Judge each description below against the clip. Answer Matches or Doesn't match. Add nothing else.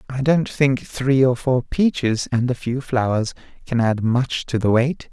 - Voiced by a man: Matches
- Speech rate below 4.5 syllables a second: Matches